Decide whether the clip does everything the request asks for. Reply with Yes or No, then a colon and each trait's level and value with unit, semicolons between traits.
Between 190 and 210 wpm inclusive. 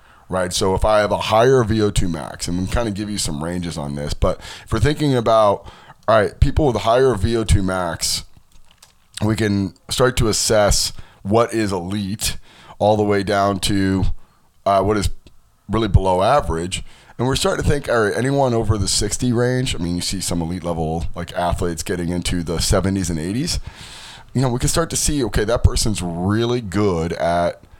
Yes: average, 195 wpm